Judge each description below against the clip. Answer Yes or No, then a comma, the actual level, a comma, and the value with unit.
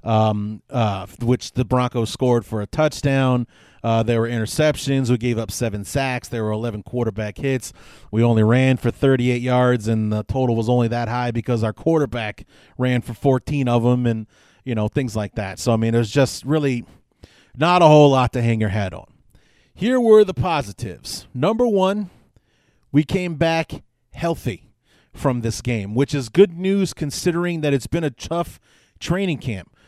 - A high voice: No, low, 125 Hz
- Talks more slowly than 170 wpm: No, average, 180 wpm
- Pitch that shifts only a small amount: No, average, 4.0 semitones